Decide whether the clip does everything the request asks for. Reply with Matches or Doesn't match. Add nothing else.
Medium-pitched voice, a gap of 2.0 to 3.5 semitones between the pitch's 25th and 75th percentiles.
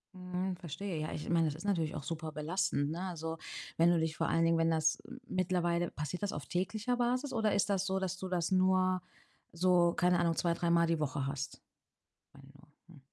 Matches